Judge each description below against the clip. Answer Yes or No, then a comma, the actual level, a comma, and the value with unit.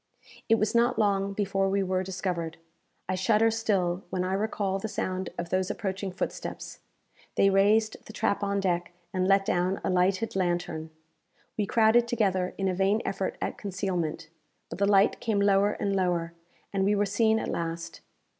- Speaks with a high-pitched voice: Yes, high, 195 Hz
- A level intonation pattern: Yes, narrow, 2.0 semitones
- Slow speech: No, average, 175 wpm